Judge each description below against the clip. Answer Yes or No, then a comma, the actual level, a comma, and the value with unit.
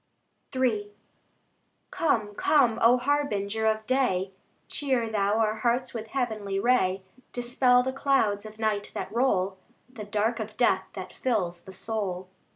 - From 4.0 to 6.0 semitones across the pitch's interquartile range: No, average, 3.5 semitones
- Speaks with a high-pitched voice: Yes, high, 220 Hz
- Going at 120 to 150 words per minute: Yes, average, 140 wpm